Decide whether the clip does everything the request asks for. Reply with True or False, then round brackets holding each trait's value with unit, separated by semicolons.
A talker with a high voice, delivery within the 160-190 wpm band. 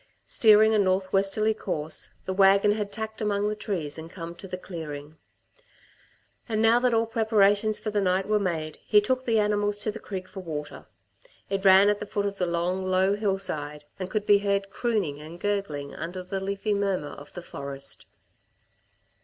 True (195 Hz; 185 wpm)